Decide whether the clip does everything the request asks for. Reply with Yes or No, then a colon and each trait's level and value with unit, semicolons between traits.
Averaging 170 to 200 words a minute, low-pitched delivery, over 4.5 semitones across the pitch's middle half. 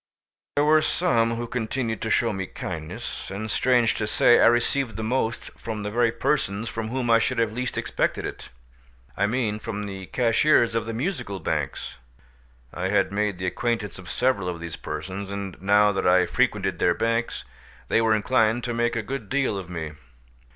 No: average, 185 wpm; low, 110 Hz; average, 3.5 semitones